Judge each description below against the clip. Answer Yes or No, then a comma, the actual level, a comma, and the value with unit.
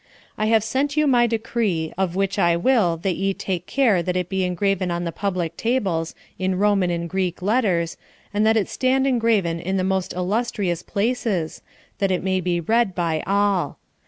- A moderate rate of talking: Yes, average, 190 wpm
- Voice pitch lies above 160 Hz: Yes, high, 190 Hz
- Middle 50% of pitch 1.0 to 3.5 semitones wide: No, average, 4.0 semitones